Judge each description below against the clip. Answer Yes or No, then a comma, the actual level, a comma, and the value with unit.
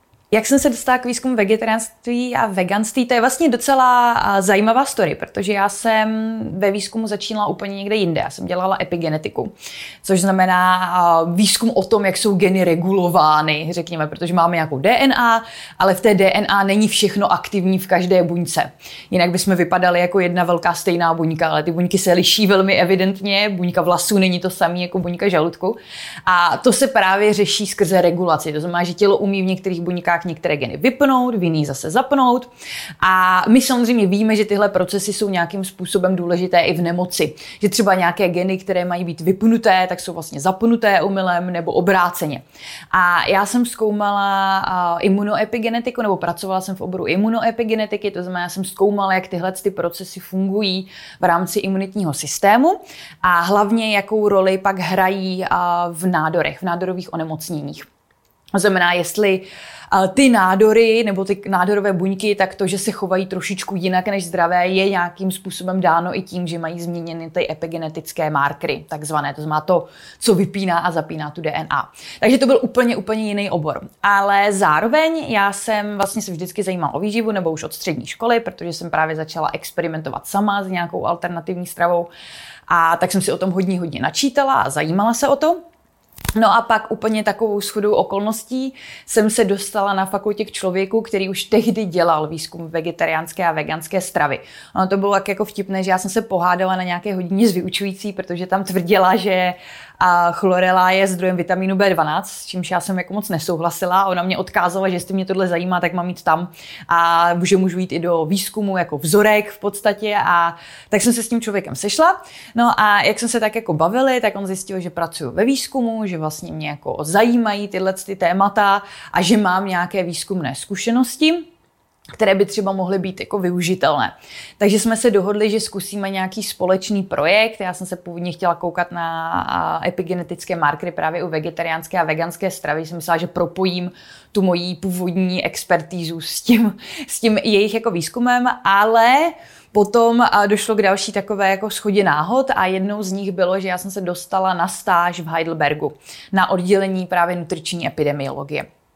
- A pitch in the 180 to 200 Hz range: Yes, high, 190 Hz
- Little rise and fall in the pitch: No, average, 3.0 semitones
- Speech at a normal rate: No, fast, 175 wpm